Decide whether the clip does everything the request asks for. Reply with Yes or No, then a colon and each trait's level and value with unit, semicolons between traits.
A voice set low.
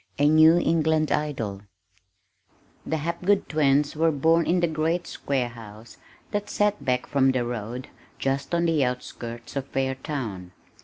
No: medium, 145 Hz